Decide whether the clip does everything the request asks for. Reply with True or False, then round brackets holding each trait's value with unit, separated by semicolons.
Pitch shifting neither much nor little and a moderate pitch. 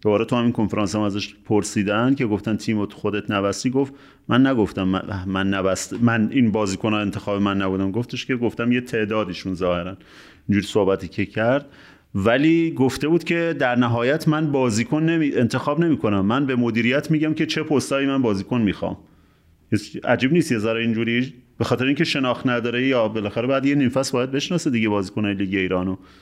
False (4.7 semitones; 115 Hz)